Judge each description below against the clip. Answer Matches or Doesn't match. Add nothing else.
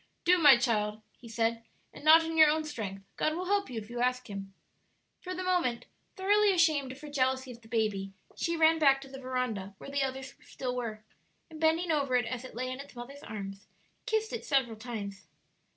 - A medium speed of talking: Doesn't match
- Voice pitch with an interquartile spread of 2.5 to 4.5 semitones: Doesn't match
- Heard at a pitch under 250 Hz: Doesn't match